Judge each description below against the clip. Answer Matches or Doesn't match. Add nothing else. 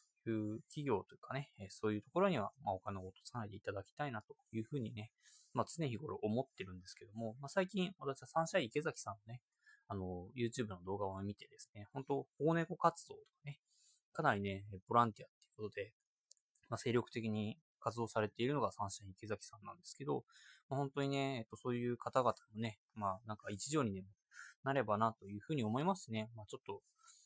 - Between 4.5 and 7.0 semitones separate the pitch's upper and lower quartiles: Matches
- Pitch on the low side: Matches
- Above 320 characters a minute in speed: Matches